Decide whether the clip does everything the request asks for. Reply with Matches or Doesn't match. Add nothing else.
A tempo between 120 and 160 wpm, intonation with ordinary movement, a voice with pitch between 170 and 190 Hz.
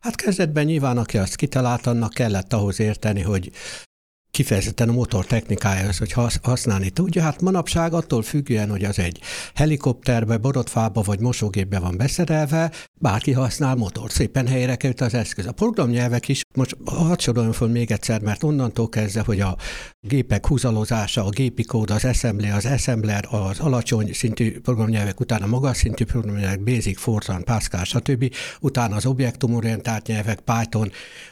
Doesn't match